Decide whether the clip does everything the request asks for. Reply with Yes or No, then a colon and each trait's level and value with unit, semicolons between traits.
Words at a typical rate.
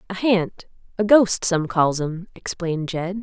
Yes: average, 165 wpm